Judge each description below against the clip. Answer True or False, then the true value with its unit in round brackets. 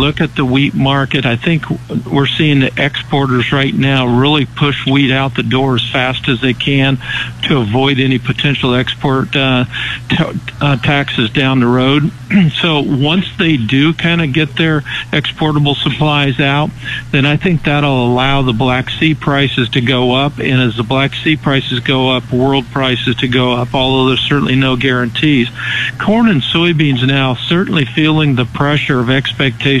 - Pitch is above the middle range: False (135 Hz)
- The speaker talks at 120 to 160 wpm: False (175 wpm)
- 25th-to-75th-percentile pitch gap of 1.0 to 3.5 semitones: True (2.5 semitones)